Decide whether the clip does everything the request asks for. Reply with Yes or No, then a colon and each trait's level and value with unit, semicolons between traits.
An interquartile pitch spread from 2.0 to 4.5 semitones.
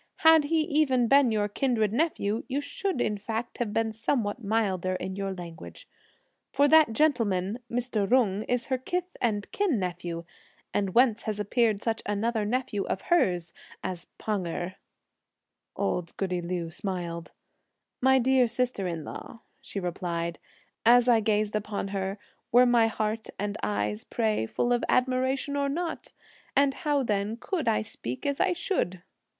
No: average, 5.2 semitones